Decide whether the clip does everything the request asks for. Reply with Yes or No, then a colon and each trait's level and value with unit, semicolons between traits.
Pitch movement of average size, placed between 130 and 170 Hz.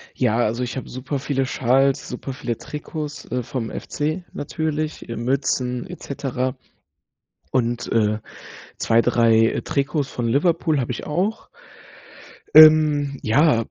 Yes: average, 3.8 semitones; low, 135 Hz